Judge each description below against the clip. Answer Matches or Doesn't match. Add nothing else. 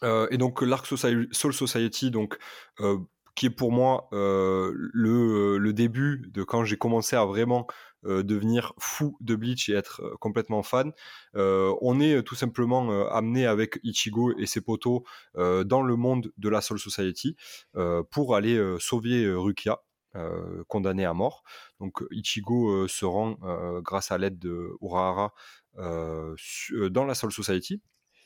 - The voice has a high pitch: Doesn't match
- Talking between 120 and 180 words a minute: Matches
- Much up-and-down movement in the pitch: Doesn't match